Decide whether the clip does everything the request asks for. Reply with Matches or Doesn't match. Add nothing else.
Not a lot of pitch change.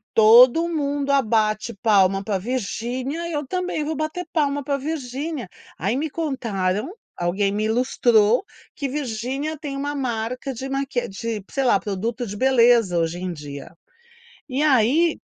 Doesn't match